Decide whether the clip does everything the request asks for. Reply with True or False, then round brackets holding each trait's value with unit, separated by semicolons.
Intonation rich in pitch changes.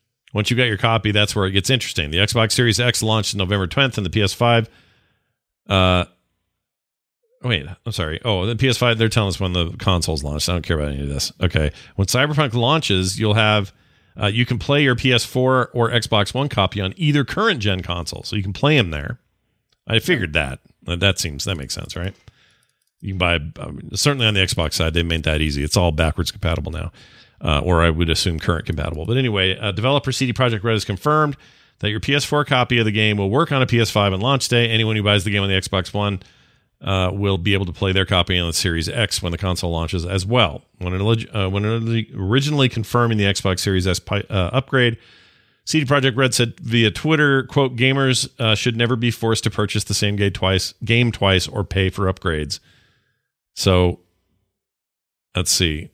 False (4.6 semitones)